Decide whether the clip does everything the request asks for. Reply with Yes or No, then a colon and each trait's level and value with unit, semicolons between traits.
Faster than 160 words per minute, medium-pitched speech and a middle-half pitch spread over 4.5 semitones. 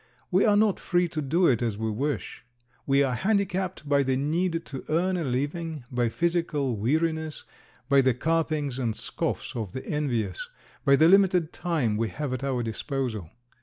Yes: average, 175 wpm; medium, 145 Hz; average, 5.0 semitones